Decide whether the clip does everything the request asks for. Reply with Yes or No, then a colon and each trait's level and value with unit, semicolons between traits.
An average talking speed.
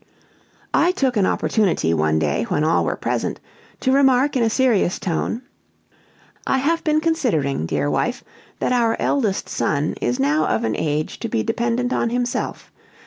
Yes: average, 165 wpm